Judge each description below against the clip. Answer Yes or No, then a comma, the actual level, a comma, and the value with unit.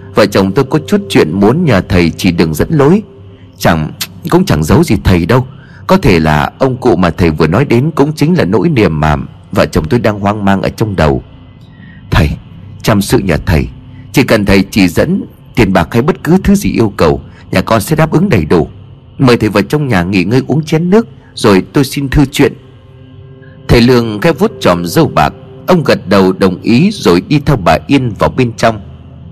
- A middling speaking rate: Yes, average, 215 wpm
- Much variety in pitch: Yes, wide, 7.2 semitones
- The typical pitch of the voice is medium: No, low, 115 Hz